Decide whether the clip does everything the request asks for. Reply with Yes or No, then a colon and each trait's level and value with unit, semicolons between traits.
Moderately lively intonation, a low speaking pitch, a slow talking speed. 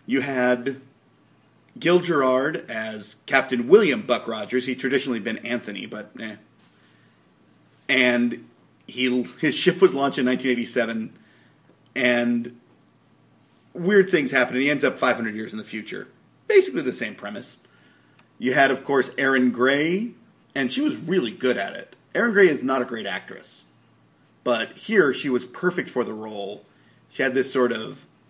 No: average, 3.2 semitones; low, 125 Hz; average, 155 wpm